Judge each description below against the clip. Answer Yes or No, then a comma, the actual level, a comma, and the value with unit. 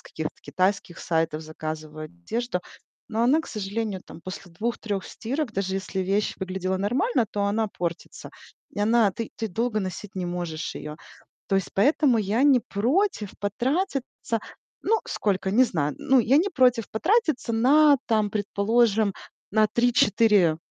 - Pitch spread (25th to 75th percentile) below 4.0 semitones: No, average, 4.4 semitones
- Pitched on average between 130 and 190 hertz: No, high, 210 Hz